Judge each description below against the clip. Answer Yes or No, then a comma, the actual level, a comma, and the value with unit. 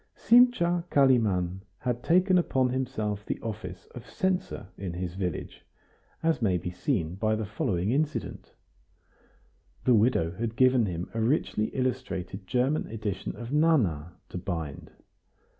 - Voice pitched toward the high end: No, low, 110 Hz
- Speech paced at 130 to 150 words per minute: Yes, slow, 135 wpm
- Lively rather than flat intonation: Yes, wide, 6.2 semitones